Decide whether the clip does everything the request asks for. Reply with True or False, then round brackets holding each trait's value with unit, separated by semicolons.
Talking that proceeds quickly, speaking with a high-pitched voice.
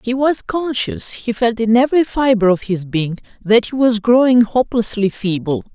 False (175 wpm; 230 Hz)